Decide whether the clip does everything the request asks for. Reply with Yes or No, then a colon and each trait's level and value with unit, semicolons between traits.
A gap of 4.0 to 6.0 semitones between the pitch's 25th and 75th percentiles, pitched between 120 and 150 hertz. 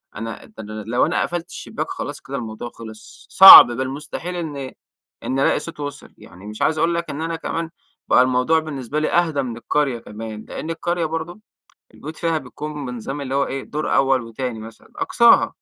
Yes: average, 5.1 semitones; medium, 140 Hz